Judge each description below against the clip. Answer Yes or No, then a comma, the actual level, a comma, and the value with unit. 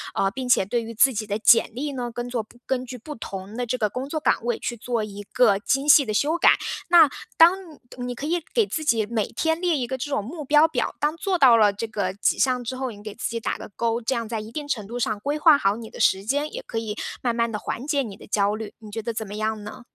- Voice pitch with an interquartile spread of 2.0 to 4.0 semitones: No, average, 4.5 semitones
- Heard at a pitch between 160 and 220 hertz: No, high, 235 Hz